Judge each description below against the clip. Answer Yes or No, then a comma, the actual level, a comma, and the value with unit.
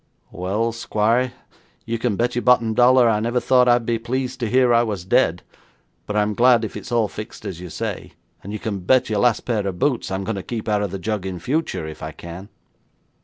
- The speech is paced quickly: Yes, fast, 230 wpm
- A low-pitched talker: Yes, low, 110 Hz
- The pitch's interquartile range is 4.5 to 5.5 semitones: No, average, 3.6 semitones